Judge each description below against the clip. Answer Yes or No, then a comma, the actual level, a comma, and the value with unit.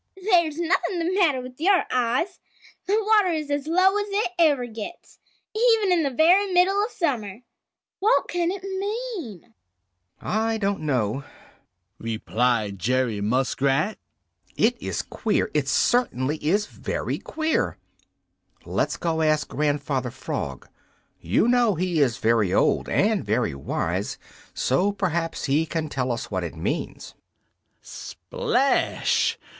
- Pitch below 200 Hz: No, high, 225 Hz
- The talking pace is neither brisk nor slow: No, slow, 130 wpm